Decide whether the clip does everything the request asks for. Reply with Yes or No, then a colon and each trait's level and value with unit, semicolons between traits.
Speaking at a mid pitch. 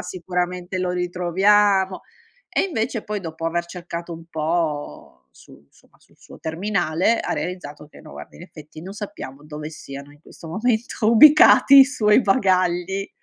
Yes: medium, 180 Hz